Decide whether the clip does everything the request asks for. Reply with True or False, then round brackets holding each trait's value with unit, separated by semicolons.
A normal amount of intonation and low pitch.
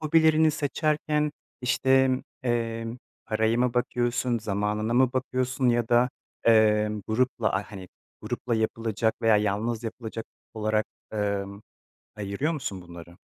True (3.2 semitones; 115 Hz)